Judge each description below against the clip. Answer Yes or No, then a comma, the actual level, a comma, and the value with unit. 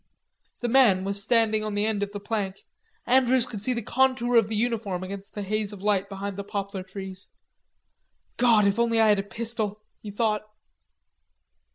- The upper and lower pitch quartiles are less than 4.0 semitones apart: Yes, narrow, 2.6 semitones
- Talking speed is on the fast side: No, average, 185 wpm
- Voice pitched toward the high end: Yes, high, 210 Hz